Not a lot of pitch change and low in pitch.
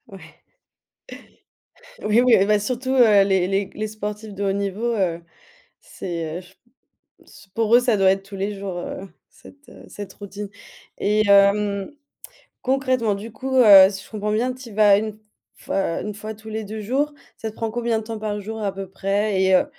No: narrow, 2.3 semitones; high, 210 Hz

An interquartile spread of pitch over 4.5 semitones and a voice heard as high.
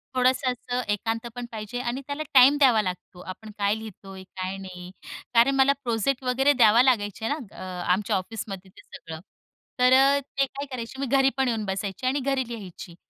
Yes: average, 5.2 semitones; high, 230 Hz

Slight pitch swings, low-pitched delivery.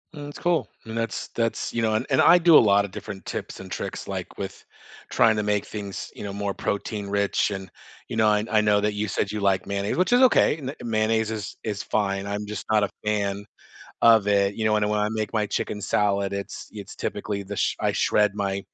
Yes: narrow, 1.7 semitones; low, 105 Hz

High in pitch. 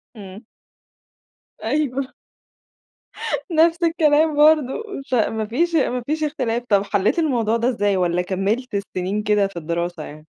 Yes: high, 230 Hz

